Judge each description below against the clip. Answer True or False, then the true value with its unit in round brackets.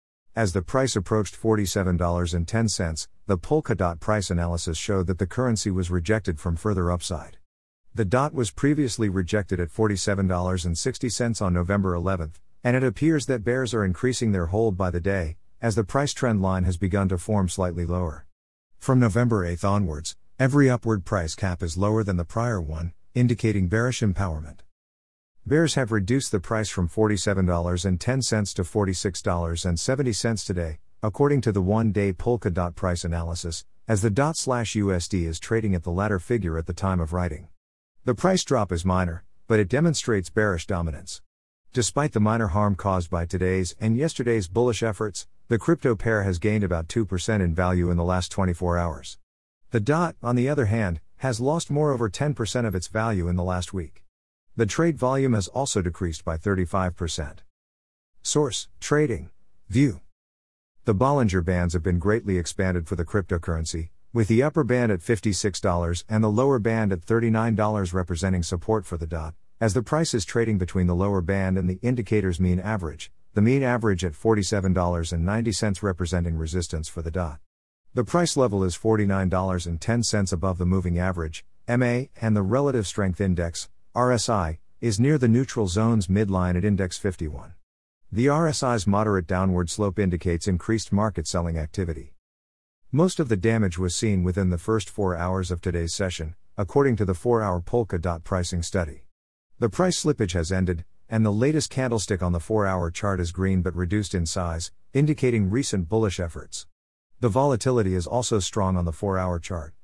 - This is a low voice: True (95 Hz)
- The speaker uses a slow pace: False (170 wpm)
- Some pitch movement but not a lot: True (4.4 semitones)